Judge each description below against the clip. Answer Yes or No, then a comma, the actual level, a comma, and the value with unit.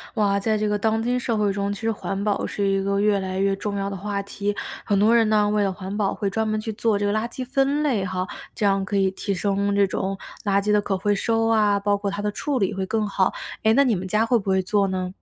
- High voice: Yes, high, 205 Hz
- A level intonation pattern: Yes, narrow, 1.7 semitones